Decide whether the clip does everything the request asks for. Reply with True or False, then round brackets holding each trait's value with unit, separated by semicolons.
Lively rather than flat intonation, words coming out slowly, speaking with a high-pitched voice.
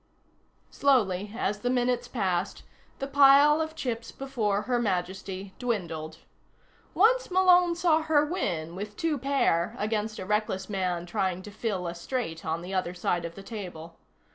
False (6.9 semitones; 155 wpm; 210 Hz)